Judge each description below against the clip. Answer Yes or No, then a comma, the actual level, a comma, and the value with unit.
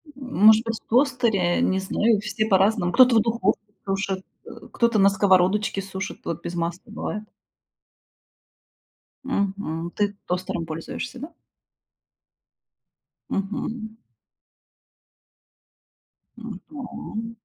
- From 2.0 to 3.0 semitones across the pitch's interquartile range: No, average, 3.4 semitones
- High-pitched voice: Yes, high, 205 Hz